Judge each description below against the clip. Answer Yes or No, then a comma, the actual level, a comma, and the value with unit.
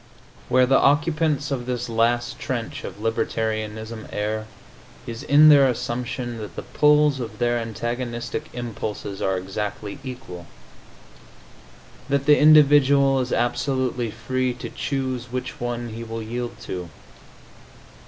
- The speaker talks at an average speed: No, slow, 125 wpm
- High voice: No, low, 120 Hz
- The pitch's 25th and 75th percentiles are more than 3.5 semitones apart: No, average, 3.0 semitones